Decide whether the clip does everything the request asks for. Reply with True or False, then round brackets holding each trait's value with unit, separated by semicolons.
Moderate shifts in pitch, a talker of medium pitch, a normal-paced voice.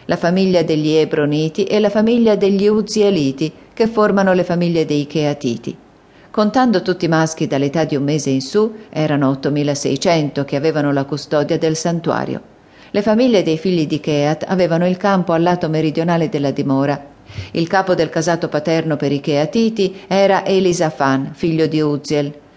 True (4.4 semitones; 160 Hz; 160 wpm)